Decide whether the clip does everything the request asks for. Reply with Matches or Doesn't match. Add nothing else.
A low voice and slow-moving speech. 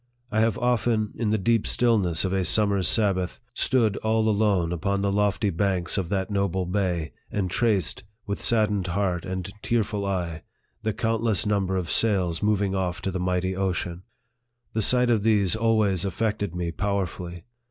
Doesn't match